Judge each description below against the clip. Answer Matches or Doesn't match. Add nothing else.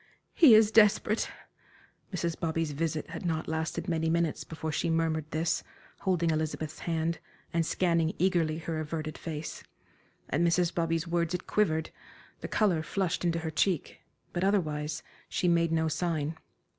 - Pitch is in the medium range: Matches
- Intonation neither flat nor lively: Doesn't match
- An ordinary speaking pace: Matches